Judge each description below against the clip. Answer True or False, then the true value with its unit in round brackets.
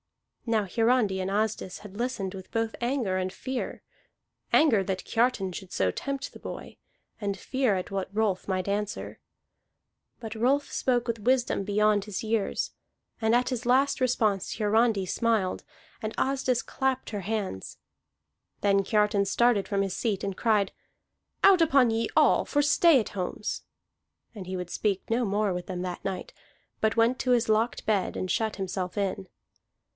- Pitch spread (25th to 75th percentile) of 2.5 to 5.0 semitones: True (3.8 semitones)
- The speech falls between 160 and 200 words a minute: True (165 wpm)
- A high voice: True (215 Hz)